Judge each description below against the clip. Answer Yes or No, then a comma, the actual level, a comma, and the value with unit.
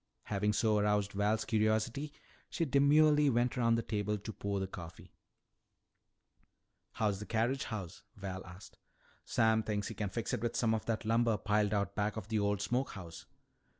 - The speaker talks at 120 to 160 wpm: No, average, 175 wpm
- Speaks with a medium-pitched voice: No, low, 110 Hz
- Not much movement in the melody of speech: Yes, narrow, 2.3 semitones